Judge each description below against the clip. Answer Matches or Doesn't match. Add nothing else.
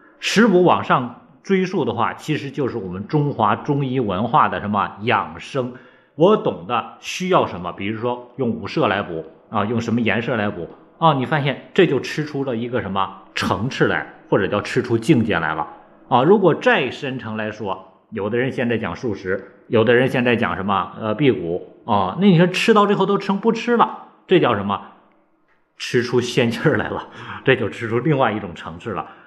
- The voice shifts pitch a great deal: Matches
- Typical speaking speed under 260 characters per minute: Doesn't match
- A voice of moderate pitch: Doesn't match